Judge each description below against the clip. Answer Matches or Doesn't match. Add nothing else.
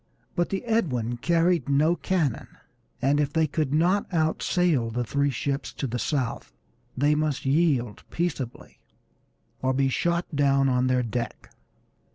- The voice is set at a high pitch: Doesn't match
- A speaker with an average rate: Matches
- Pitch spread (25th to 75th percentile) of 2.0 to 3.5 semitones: Doesn't match